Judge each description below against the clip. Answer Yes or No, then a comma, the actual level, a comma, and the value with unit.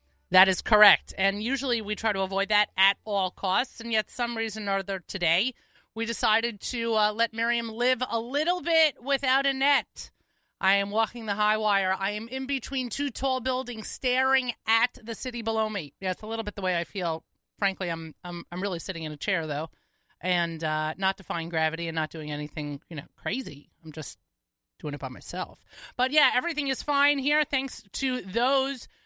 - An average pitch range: No, wide, 5.8 semitones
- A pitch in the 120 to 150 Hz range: No, high, 215 Hz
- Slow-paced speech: No, average, 200 wpm